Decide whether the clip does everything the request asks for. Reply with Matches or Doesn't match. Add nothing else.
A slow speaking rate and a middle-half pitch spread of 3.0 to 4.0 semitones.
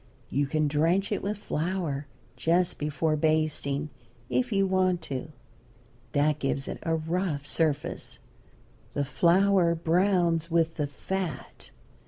Matches